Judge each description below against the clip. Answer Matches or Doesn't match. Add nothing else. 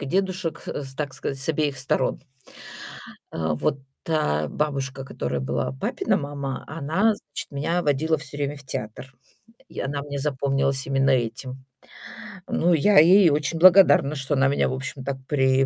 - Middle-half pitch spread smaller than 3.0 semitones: Matches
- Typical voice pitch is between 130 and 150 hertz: Matches